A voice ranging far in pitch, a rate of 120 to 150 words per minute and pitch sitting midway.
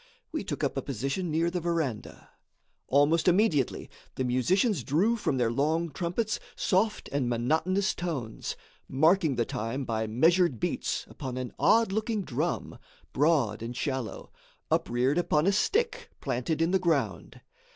Yes: wide, 6.3 semitones; average, 145 wpm; medium, 155 Hz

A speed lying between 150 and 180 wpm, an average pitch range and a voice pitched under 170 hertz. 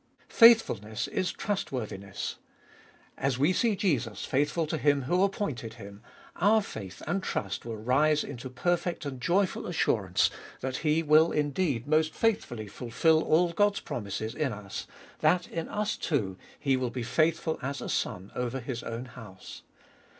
No: average, 155 wpm; wide, 6.4 semitones; medium, 140 Hz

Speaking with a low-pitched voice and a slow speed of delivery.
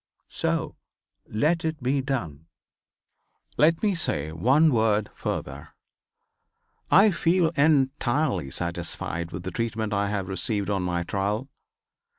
Yes: low, 110 Hz; slow, 120 wpm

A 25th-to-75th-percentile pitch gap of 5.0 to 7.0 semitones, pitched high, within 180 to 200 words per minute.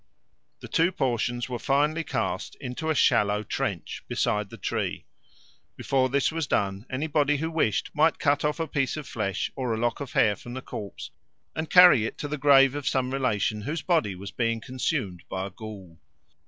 No: wide, 5.5 semitones; low, 130 Hz; average, 190 wpm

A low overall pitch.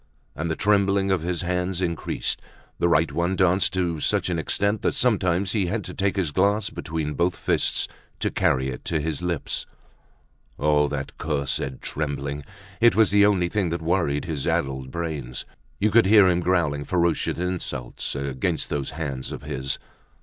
Yes: very low, 85 Hz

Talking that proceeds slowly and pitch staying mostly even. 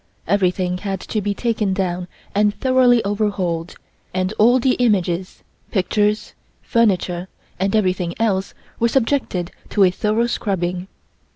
No: slow, 125 wpm; average, 3.5 semitones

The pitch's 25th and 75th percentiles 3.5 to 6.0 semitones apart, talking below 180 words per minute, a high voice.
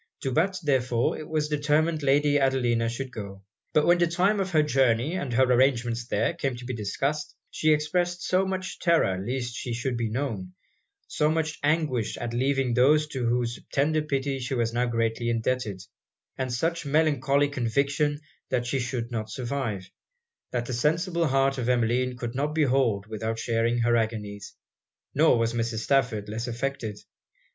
No: average, 4.2 semitones; average, 170 wpm; low, 130 Hz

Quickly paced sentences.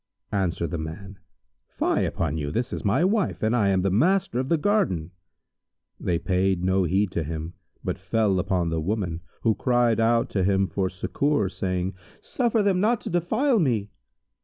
No: average, 180 wpm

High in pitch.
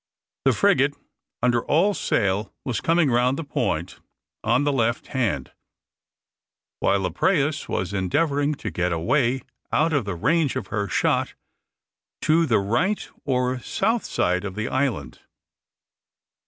No: low, 125 Hz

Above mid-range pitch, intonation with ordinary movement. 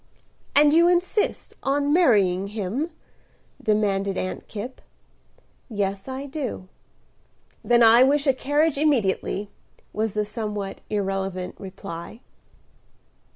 No: high, 220 Hz; wide, 6.2 semitones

